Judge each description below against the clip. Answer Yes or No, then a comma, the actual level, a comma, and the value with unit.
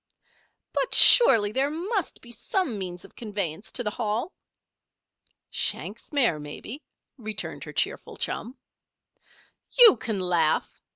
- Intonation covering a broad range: Yes, wide, 6.4 semitones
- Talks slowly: Yes, slow, 120 wpm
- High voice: Yes, high, 225 Hz